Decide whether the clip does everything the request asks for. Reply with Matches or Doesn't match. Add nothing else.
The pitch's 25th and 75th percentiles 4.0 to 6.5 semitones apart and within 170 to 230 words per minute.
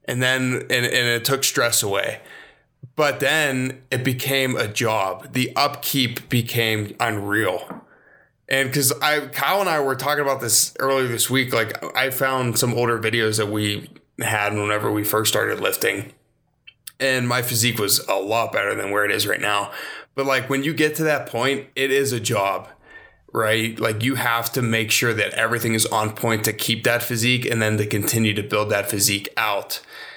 Doesn't match